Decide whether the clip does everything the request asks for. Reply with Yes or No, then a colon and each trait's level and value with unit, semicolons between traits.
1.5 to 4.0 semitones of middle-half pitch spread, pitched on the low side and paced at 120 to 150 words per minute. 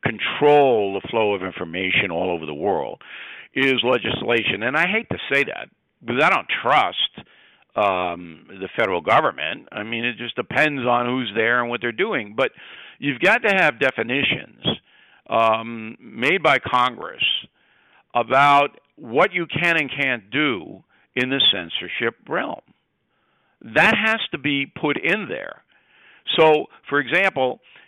No: average, 4.7 semitones; low, 130 Hz; average, 145 wpm